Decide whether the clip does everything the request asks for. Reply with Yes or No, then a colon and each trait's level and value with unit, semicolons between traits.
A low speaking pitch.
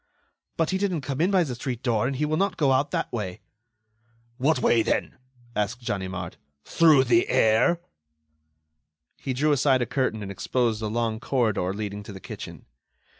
Yes: low, 125 Hz